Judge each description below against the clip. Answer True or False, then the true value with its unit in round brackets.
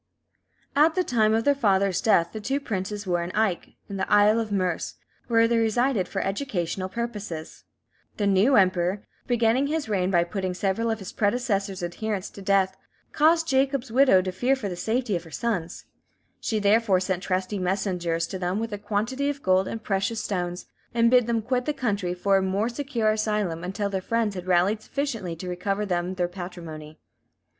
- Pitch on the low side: False (205 Hz)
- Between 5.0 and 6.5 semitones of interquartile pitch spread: False (3.9 semitones)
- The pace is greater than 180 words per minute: True (190 wpm)